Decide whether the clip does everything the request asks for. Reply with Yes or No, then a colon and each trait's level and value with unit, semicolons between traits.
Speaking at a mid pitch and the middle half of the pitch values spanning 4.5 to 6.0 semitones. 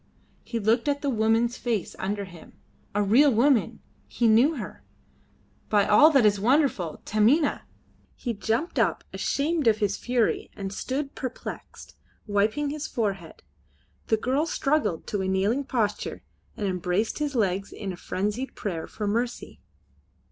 No: high, 225 Hz; average, 5.0 semitones